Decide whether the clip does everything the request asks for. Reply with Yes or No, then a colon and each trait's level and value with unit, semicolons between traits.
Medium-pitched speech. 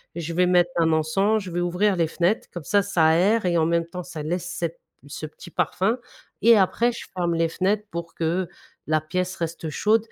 Yes: medium, 175 Hz